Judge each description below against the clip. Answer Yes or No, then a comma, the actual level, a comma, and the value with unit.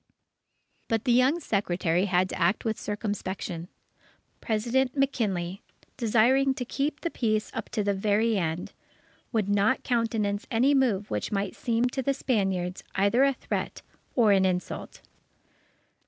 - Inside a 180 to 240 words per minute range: No, average, 140 wpm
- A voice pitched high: Yes, high, 215 Hz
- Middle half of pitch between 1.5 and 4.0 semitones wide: No, average, 4.5 semitones